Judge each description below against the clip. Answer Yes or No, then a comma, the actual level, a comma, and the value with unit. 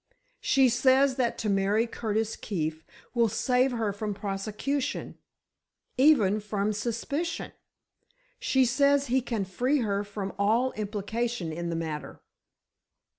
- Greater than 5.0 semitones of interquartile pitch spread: No, average, 4.1 semitones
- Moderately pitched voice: No, high, 220 Hz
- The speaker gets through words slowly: Yes, slow, 120 wpm